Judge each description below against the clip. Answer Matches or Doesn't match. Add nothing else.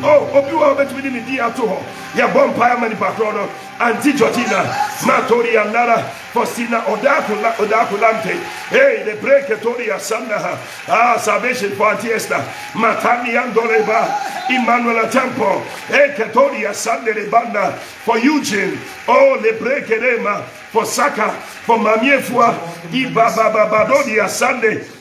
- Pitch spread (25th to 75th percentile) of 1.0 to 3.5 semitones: Doesn't match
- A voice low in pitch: Doesn't match